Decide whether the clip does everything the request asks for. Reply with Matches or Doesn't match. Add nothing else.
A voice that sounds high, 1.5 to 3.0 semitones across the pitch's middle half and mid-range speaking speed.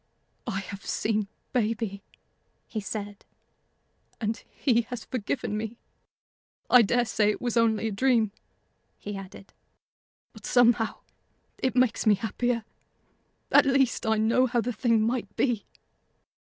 Doesn't match